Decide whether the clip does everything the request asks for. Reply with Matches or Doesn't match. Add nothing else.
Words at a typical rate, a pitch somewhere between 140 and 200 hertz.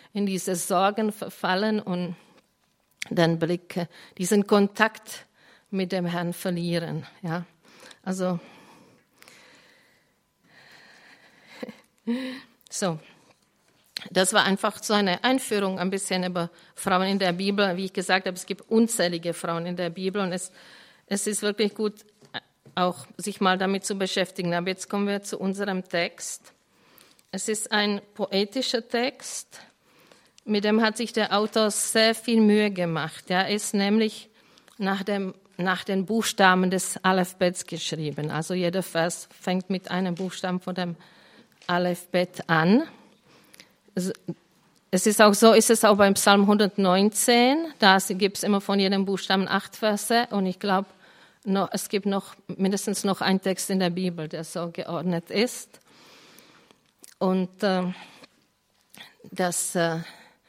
Matches